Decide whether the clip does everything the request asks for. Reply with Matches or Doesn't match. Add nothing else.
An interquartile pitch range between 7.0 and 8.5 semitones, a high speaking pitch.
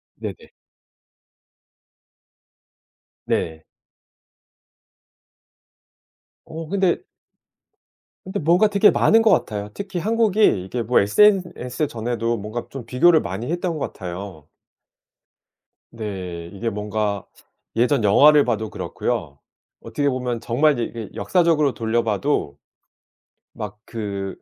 Doesn't match